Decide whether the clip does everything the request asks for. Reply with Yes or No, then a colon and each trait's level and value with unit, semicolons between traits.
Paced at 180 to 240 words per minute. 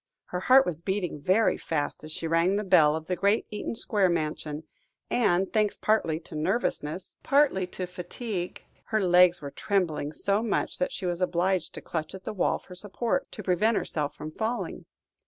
Yes: average, 185 wpm